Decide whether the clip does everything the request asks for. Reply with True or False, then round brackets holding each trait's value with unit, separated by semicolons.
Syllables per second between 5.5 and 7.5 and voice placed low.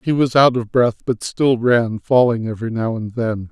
False (4.8 syllables/s; 120 Hz)